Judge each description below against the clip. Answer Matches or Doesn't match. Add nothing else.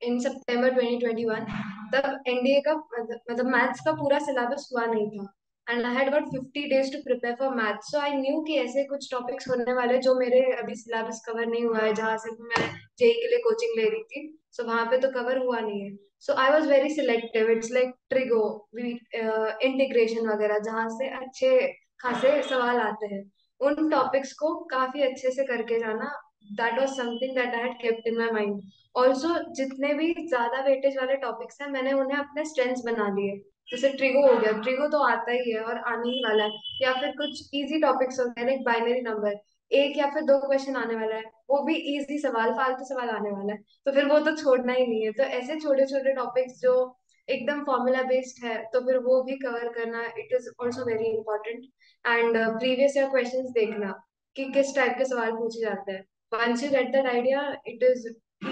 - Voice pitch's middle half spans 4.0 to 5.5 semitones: Doesn't match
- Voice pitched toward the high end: Matches